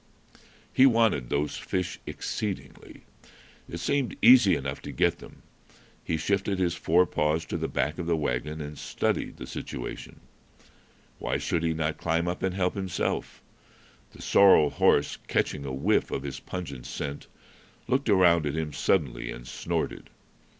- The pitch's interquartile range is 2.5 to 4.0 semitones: No, average, 4.4 semitones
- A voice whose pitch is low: Yes, very low, 80 Hz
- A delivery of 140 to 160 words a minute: Yes, average, 155 wpm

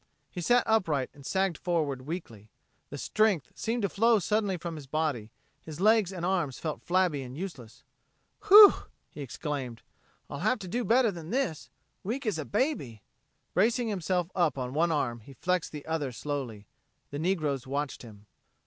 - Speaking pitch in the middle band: Yes, medium, 160 Hz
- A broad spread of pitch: Yes, wide, 6.2 semitones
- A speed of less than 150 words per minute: No, average, 165 wpm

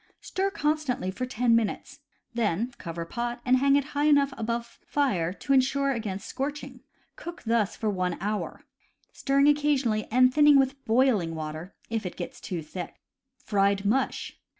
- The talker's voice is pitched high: Yes, high, 240 Hz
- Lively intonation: Yes, wide, 5.8 semitones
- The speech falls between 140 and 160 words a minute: Yes, average, 155 wpm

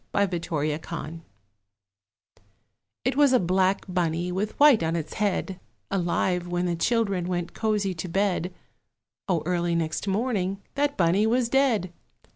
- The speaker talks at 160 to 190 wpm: No, slow, 135 wpm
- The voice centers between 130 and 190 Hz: Yes, medium, 185 Hz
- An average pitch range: Yes, average, 3.6 semitones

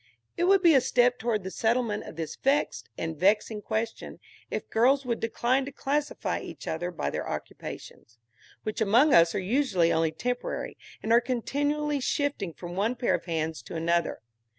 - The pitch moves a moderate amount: No, wide, 7.3 semitones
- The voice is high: Yes, high, 225 Hz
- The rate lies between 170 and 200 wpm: Yes, average, 175 wpm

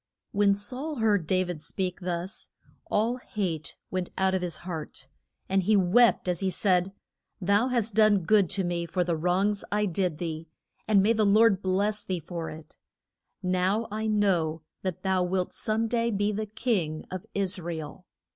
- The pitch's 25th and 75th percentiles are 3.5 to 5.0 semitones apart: No, average, 3.0 semitones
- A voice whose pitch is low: No, high, 190 Hz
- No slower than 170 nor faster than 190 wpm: Yes, average, 180 wpm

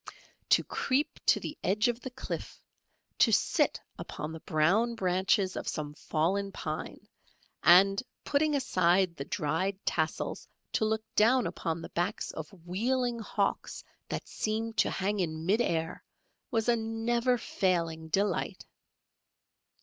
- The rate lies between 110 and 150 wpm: Yes, slow, 135 wpm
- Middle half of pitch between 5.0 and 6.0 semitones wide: Yes, average, 5.3 semitones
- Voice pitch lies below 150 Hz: No, high, 195 Hz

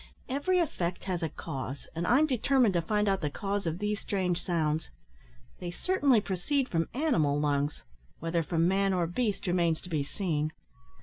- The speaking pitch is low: No, medium, 180 Hz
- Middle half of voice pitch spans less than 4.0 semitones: No, average, 4.4 semitones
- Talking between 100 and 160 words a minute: No, average, 175 wpm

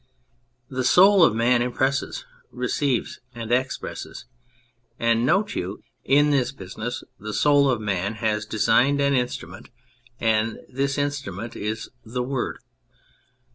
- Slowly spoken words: Yes, slow, 125 wpm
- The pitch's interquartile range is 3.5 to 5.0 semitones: Yes, average, 4.2 semitones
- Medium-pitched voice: No, low, 125 Hz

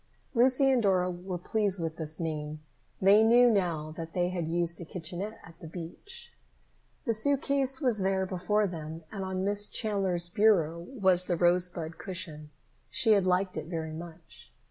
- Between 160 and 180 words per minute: Yes, average, 170 wpm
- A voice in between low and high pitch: Yes, medium, 180 Hz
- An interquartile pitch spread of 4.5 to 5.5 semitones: No, average, 3.9 semitones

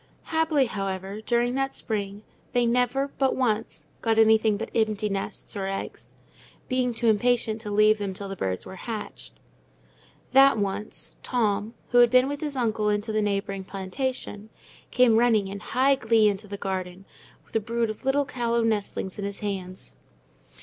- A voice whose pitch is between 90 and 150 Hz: No, high, 220 Hz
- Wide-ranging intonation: No, average, 3.4 semitones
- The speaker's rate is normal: Yes, average, 165 wpm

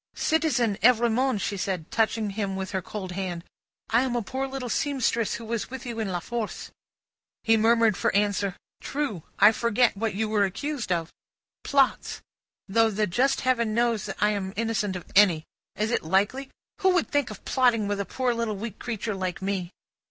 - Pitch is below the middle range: No, high, 220 Hz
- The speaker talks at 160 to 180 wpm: No, average, 190 wpm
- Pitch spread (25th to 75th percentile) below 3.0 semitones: No, average, 3.5 semitones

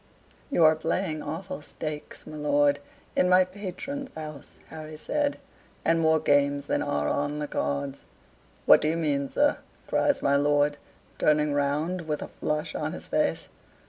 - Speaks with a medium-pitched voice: Yes, medium, 150 Hz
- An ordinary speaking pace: Yes, average, 160 wpm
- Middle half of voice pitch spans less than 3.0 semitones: Yes, narrow, 2.6 semitones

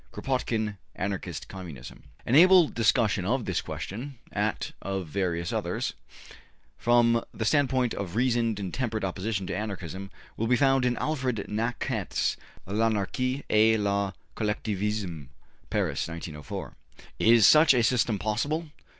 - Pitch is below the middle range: Yes, low, 110 Hz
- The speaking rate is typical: No, slow, 125 wpm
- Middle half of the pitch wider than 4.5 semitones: No, average, 4.2 semitones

